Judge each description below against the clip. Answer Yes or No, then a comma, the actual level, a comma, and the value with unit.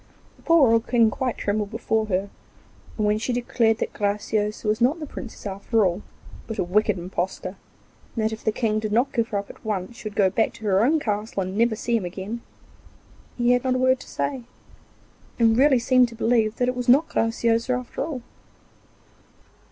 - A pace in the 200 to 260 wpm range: Yes, fast, 205 wpm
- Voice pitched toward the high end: Yes, high, 225 Hz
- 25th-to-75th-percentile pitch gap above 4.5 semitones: No, average, 2.8 semitones